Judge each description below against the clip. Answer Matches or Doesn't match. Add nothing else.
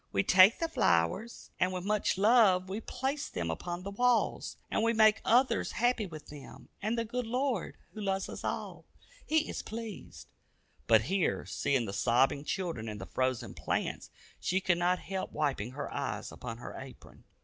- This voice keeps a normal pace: Matches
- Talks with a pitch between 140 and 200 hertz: Matches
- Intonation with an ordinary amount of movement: Doesn't match